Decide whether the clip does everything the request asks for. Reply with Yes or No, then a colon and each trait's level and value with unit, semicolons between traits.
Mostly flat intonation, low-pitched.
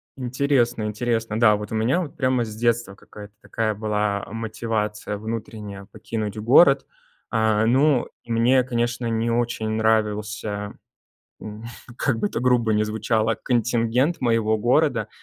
Yes: narrow, 2.1 semitones; low, 115 Hz